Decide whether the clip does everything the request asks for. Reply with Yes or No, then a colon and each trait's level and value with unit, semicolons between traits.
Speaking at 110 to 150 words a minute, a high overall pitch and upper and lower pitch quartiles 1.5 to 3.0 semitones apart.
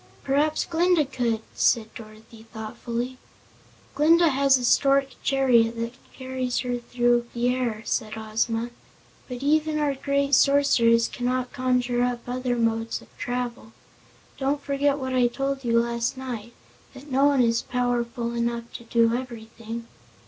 Yes: average, 140 wpm; high, 245 Hz; narrow, 2.6 semitones